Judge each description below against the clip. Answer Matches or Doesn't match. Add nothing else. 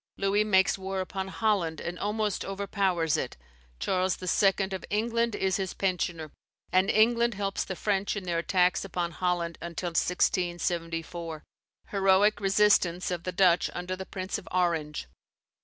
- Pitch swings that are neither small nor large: Doesn't match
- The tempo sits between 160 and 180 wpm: Doesn't match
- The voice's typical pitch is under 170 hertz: Doesn't match